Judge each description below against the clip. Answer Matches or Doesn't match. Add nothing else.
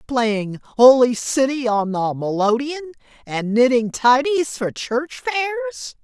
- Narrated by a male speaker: Doesn't match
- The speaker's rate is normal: Doesn't match